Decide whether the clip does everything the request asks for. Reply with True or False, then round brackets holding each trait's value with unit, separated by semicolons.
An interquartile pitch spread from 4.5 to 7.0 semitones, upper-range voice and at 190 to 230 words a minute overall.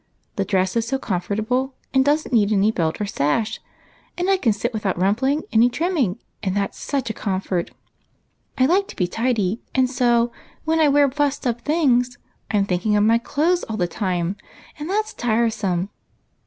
True (5.3 semitones; 230 Hz; 195 wpm)